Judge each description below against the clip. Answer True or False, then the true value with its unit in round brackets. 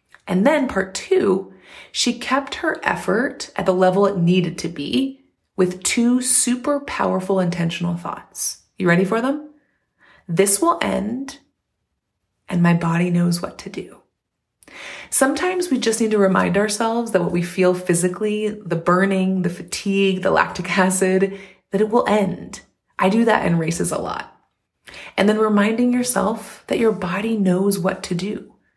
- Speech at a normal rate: True (160 wpm)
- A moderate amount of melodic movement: True (4.4 semitones)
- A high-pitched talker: True (195 Hz)